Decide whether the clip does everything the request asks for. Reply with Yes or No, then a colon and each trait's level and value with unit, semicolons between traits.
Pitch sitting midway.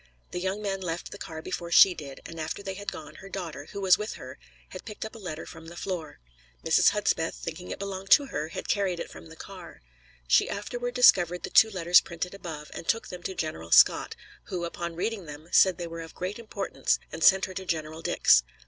Yes: medium, 180 Hz